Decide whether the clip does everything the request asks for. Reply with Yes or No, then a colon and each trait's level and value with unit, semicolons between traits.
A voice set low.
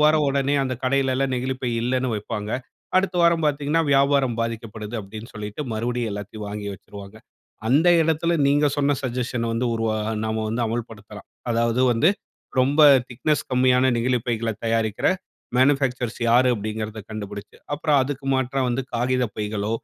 Yes: low, 125 Hz